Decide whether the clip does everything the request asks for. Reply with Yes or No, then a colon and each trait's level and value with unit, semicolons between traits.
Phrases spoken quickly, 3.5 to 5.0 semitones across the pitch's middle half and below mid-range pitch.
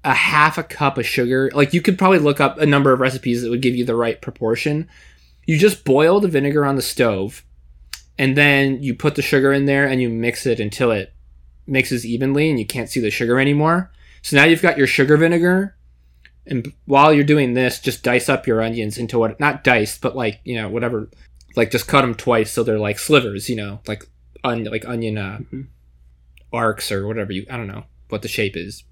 Yes: fast, 220 wpm; average, 4.6 semitones; low, 125 Hz